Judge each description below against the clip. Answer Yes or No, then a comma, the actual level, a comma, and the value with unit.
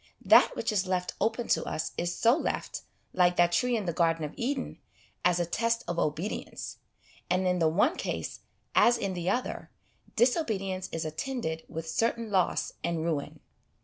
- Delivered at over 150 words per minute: Yes, average, 175 wpm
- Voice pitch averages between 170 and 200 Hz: Yes, medium, 185 Hz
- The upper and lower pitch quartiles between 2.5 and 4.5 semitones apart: No, wide, 5.4 semitones